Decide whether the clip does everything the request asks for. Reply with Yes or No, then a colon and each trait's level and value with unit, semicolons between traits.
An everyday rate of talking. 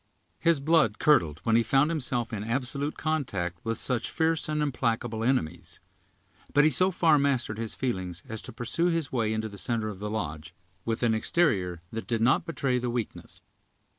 Yes: average, 185 wpm